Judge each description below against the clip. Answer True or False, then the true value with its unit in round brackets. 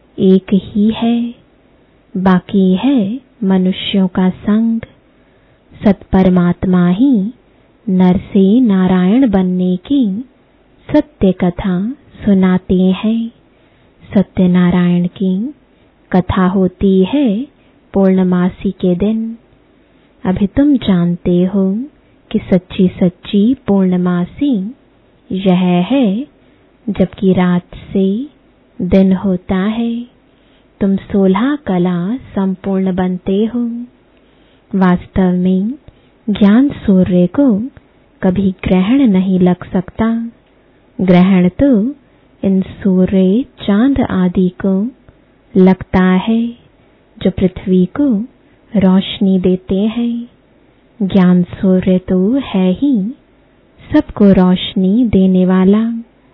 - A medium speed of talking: False (90 wpm)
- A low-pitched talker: False (195 Hz)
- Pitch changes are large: False (3.7 semitones)